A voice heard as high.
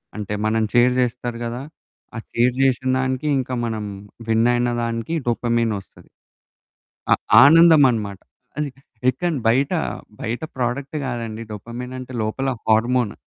No: low, 120 Hz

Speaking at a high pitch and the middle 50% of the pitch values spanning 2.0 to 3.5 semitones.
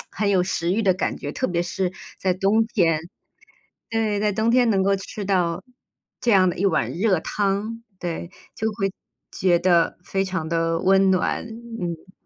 Yes: high, 195 Hz; average, 3.1 semitones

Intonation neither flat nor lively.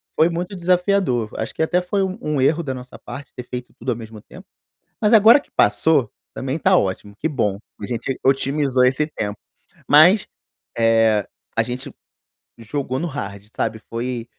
No: wide, 6.0 semitones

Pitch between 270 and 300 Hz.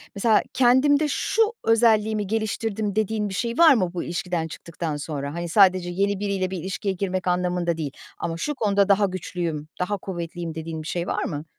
No: medium, 185 Hz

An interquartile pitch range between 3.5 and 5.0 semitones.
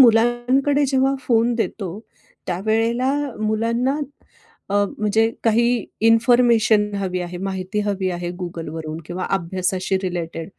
Yes: average, 4.5 semitones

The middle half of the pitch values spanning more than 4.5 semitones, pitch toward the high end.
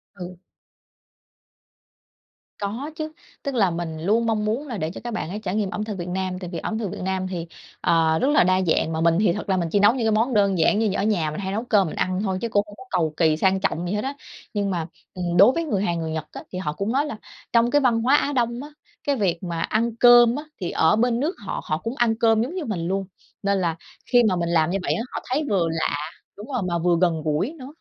Yes: average, 5.1 semitones; high, 200 Hz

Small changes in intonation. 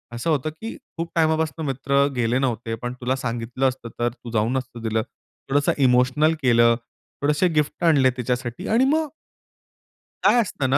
No: average, 4.2 semitones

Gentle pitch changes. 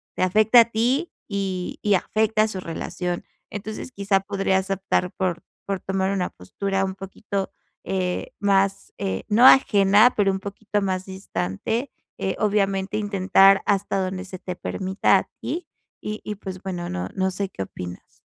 Yes: narrow, 1.8 semitones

